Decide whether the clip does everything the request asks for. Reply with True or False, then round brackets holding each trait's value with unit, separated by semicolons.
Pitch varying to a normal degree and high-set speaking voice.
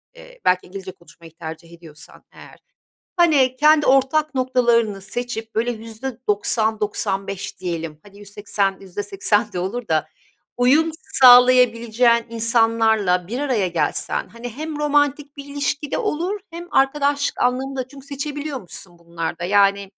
False (5.8 semitones; 230 Hz)